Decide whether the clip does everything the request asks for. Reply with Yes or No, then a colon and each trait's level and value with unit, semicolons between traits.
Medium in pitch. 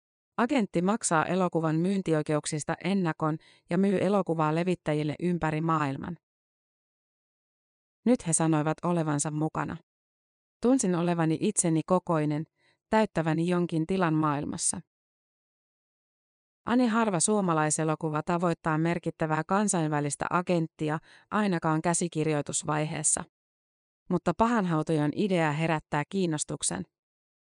Yes: medium, 165 Hz